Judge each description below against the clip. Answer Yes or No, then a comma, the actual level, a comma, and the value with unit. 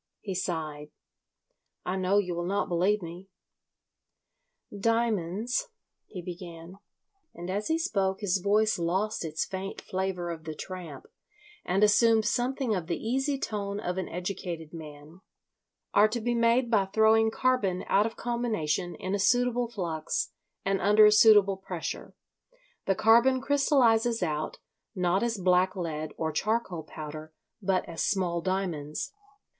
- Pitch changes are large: No, average, 4.3 semitones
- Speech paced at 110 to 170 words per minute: Yes, average, 140 wpm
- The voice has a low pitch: No, high, 195 Hz